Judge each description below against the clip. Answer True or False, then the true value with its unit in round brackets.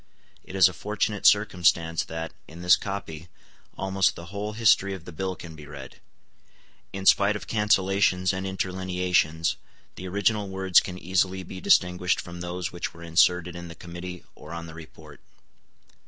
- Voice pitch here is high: False (90 Hz)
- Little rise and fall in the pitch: True (2.2 semitones)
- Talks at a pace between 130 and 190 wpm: True (165 wpm)